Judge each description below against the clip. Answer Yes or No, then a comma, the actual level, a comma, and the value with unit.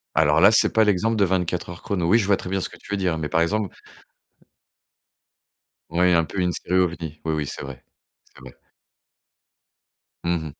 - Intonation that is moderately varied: Yes, average, 3.2 semitones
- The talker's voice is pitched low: Yes, very low, 90 Hz